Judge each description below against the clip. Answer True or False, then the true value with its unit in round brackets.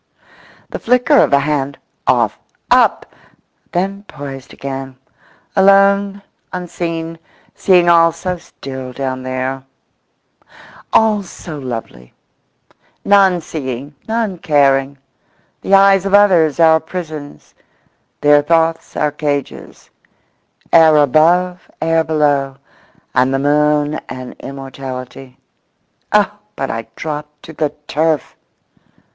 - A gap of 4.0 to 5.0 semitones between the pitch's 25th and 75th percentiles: True (4.6 semitones)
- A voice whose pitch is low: False (155 Hz)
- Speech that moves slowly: True (105 wpm)